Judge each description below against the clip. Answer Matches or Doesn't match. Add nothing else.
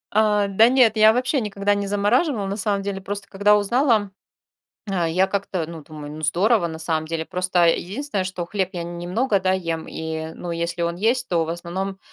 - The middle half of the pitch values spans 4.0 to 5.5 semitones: Doesn't match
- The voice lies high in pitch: Matches